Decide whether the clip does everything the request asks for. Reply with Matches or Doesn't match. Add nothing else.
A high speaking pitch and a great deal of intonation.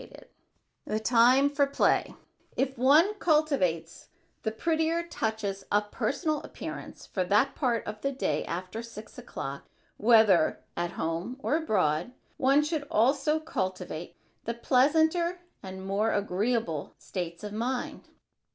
Matches